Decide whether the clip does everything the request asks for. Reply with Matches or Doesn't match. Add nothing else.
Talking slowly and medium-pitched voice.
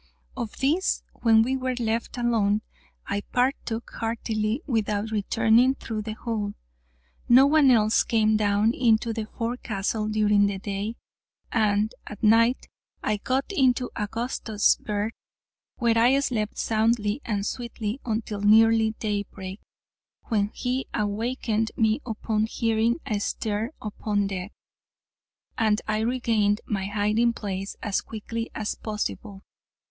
Doesn't match